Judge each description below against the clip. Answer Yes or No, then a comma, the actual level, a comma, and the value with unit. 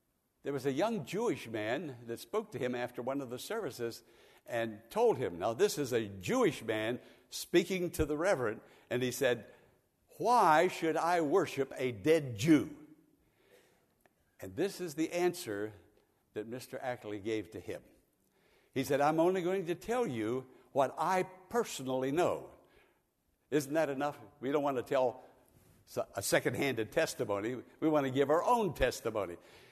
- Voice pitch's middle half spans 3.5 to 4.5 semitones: No, wide, 5.4 semitones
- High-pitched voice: No, medium, 140 Hz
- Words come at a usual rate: Yes, average, 160 wpm